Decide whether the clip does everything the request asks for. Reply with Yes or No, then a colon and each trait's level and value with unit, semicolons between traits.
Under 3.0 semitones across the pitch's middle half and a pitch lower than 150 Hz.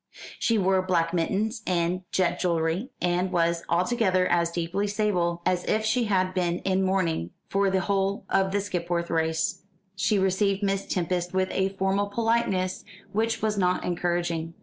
No: narrow, 2.4 semitones; medium, 185 Hz